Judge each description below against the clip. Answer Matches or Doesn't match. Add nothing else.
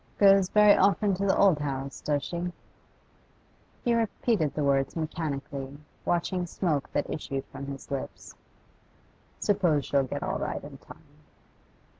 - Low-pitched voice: Doesn't match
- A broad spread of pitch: Matches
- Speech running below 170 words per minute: Matches